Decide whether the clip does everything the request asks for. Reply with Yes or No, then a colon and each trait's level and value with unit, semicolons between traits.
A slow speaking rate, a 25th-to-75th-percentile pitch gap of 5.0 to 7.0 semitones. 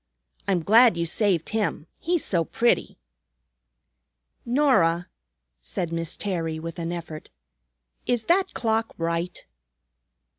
Yes: slow, 110 wpm; wide, 5.4 semitones